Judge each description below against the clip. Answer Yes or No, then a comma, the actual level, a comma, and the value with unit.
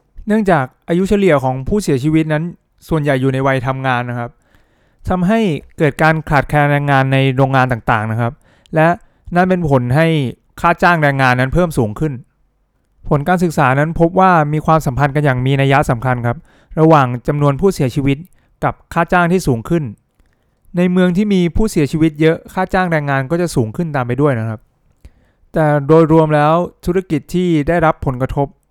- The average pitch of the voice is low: No, medium, 150 Hz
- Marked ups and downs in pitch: No, average, 4.3 semitones